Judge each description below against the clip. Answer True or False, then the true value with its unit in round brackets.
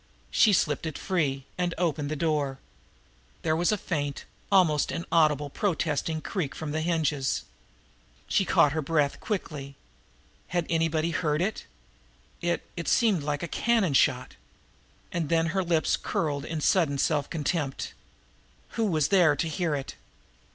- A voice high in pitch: False (160 Hz)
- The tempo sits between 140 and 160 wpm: True (145 wpm)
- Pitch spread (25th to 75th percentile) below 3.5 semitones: True (2.9 semitones)